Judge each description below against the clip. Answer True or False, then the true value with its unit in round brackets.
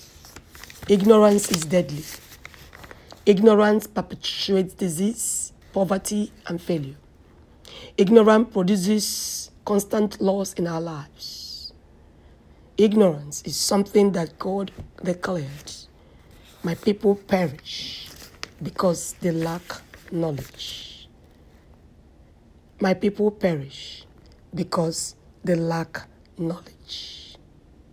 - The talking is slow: True (75 wpm)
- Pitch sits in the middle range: True (175 Hz)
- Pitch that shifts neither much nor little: False (6.7 semitones)